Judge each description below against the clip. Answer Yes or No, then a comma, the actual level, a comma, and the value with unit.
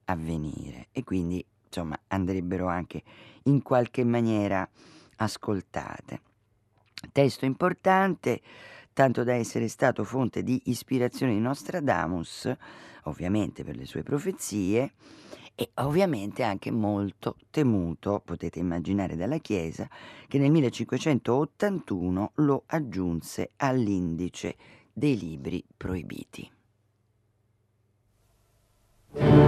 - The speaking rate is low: Yes, slow, 90 wpm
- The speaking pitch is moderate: No, low, 110 Hz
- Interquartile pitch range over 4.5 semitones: Yes, wide, 5.5 semitones